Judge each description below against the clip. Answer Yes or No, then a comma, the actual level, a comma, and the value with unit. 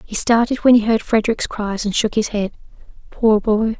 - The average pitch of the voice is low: No, high, 220 Hz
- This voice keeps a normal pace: Yes, average, 190 wpm